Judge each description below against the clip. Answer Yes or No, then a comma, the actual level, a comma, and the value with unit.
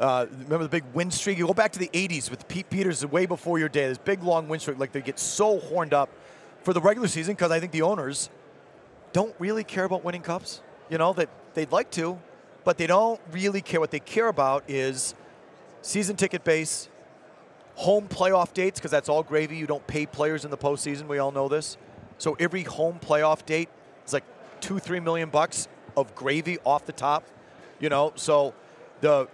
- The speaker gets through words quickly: Yes, fast, 210 wpm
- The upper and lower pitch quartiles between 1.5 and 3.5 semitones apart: No, average, 3.9 semitones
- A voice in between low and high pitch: Yes, medium, 165 Hz